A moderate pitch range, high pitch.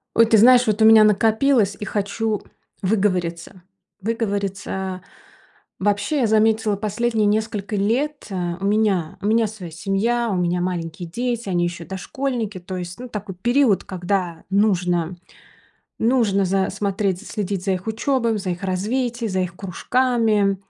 Yes: average, 3.2 semitones; high, 205 Hz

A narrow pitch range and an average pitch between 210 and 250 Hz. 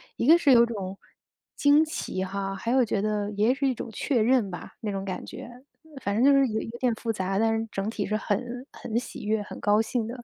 No: average, 3.4 semitones; high, 220 Hz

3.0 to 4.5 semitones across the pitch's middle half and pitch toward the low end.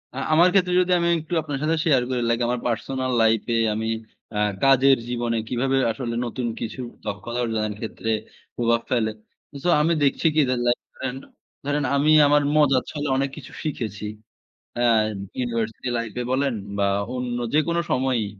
Yes: average, 3.7 semitones; low, 125 Hz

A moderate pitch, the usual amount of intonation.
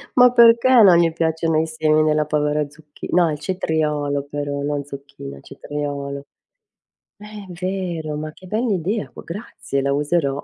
Yes: medium, 155 Hz; average, 3.4 semitones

